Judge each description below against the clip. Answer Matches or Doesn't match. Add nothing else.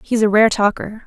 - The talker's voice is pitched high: Matches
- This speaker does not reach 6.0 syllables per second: Matches